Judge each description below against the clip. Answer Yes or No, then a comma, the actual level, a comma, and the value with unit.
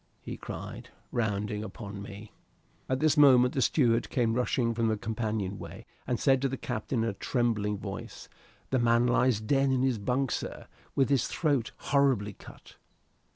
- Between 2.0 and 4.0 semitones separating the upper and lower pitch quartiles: Yes, average, 3.4 semitones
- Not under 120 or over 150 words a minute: No, average, 170 wpm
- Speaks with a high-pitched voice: No, low, 120 Hz